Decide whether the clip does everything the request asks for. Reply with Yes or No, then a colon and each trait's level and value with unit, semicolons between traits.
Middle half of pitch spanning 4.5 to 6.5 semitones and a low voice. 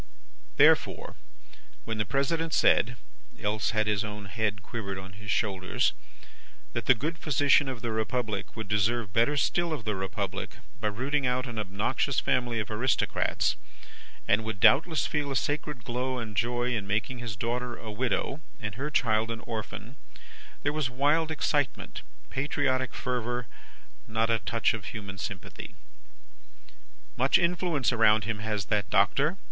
No: average, 4.0 semitones; low, 115 Hz